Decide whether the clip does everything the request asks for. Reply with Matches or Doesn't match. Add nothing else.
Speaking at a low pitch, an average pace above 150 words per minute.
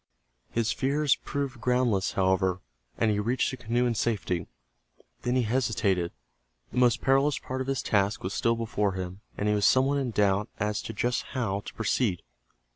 Matches